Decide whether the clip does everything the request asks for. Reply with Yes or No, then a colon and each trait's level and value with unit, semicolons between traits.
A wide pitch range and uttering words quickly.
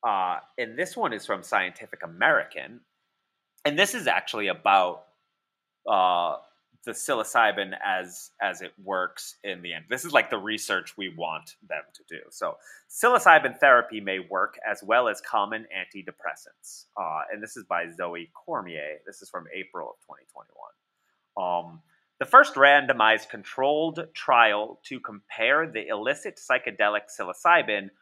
No: wide, 6.6 semitones; average, 145 wpm